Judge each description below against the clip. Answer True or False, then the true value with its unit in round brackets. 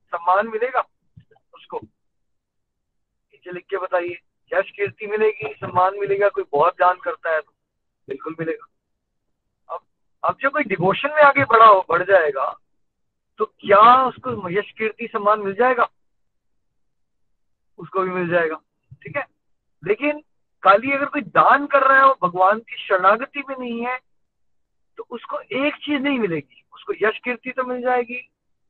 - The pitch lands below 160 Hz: False (220 Hz)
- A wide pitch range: True (6.5 semitones)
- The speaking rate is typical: True (150 wpm)